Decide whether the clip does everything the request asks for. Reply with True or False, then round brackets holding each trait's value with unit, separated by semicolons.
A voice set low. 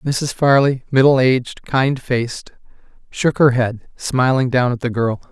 True (130 Hz)